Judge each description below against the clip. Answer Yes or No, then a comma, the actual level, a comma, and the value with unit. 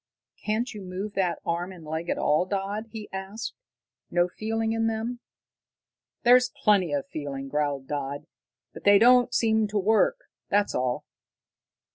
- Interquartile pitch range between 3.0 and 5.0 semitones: No, wide, 5.5 semitones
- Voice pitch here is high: Yes, high, 200 Hz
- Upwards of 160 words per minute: No, average, 150 wpm